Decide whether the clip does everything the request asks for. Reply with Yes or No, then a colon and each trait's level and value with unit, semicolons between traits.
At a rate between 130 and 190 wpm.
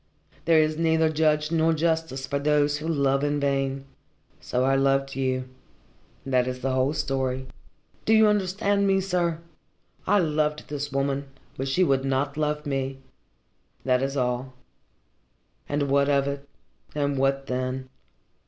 Yes: average, 150 wpm